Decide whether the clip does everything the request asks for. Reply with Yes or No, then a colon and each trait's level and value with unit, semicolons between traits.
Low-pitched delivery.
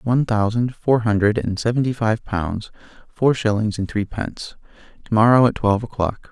Yes: low, 110 Hz